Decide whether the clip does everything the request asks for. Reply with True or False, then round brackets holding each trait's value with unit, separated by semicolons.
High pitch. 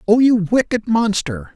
True (200 Hz)